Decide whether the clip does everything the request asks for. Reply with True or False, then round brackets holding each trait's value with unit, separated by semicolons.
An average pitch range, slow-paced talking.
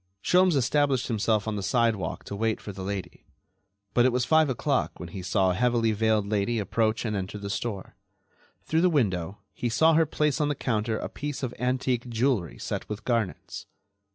False (4.3 semitones; 195 wpm)